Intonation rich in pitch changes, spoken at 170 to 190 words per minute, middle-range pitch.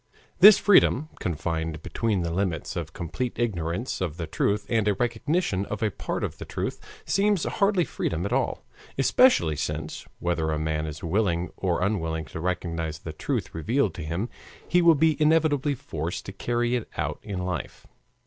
No: wide, 7.6 semitones; average, 175 wpm; very low, 95 Hz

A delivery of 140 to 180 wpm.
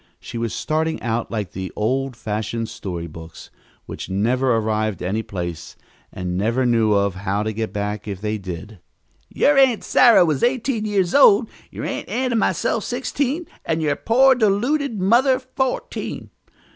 Yes: average, 160 wpm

